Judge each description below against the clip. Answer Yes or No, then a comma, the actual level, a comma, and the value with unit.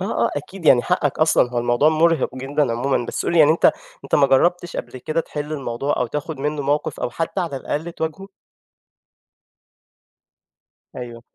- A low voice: No, medium, 150 Hz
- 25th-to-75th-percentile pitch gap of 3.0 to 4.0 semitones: Yes, average, 3.7 semitones